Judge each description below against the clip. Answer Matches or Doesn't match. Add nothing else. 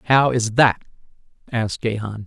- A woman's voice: Doesn't match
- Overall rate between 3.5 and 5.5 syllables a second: Matches